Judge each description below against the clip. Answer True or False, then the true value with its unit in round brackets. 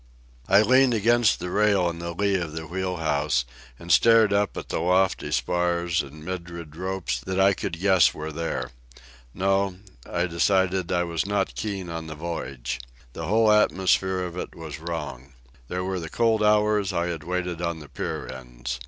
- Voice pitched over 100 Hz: False (90 Hz)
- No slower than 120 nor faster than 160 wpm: False (180 wpm)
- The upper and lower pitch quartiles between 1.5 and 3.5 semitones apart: True (3.1 semitones)